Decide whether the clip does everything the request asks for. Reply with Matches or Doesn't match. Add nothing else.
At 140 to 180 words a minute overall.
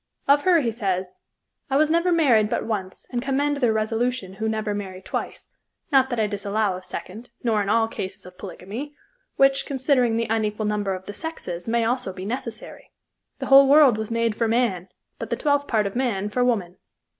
Doesn't match